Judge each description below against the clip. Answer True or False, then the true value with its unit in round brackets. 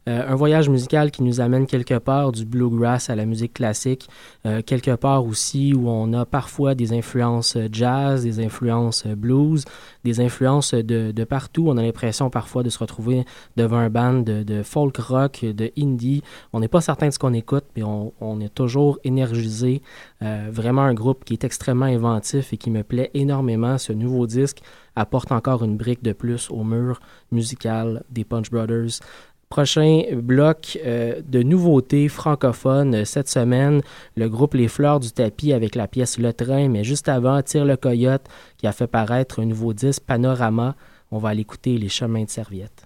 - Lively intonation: False (2.9 semitones)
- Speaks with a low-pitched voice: True (125 Hz)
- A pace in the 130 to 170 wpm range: False (185 wpm)